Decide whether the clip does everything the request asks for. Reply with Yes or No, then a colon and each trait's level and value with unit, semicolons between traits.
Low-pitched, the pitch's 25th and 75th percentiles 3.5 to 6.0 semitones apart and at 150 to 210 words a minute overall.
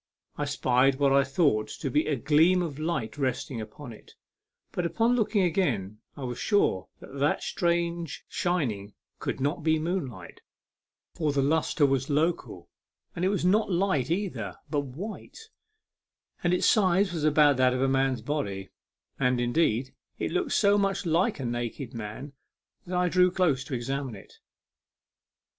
No: medium, 145 Hz; wide, 5.5 semitones; average, 160 wpm